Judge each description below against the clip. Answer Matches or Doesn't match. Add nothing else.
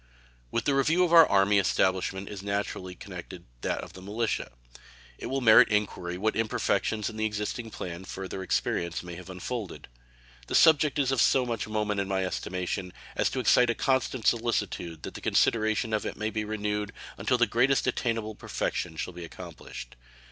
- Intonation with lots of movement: Doesn't match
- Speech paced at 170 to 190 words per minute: Matches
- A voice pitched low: Matches